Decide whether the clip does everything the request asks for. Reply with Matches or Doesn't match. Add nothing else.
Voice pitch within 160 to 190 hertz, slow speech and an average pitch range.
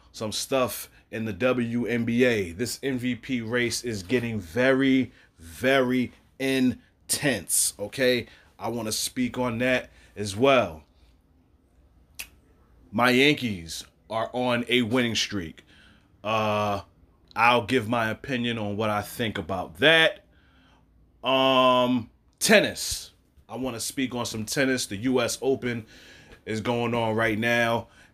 Doesn't match